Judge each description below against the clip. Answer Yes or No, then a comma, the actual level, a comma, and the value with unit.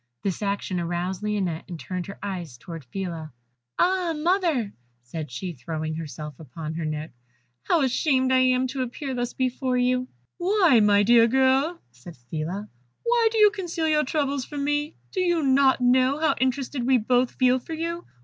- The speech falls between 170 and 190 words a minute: Yes, average, 175 wpm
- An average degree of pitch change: No, wide, 8.7 semitones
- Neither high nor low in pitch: No, very high, 250 Hz